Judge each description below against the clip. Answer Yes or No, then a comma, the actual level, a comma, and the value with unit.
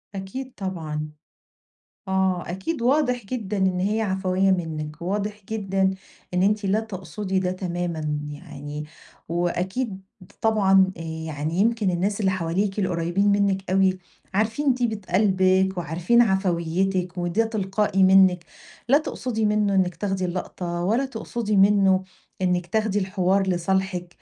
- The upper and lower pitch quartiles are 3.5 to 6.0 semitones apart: No, average, 2.7 semitones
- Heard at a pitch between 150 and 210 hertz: Yes, high, 190 Hz